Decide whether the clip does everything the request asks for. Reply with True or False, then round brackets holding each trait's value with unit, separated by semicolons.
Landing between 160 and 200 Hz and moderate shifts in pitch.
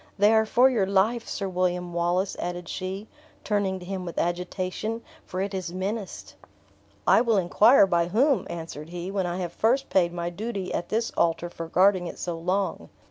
True (185 Hz; 3.0 semitones)